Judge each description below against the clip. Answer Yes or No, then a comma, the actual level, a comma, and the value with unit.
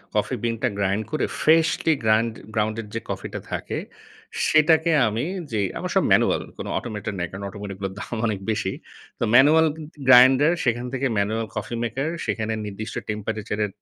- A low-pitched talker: Yes, low, 110 Hz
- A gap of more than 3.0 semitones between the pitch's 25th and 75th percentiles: Yes, average, 4.1 semitones